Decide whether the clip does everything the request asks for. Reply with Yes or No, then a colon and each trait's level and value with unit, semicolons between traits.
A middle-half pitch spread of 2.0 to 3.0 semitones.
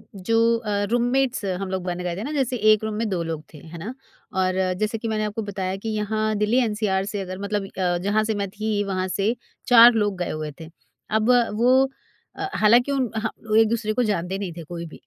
No: average, 3.4 semitones